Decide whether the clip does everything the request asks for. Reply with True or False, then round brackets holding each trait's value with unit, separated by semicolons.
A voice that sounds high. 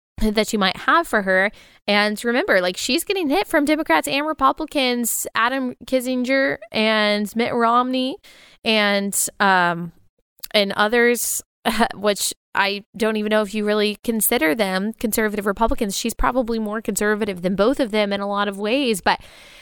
True (220 Hz)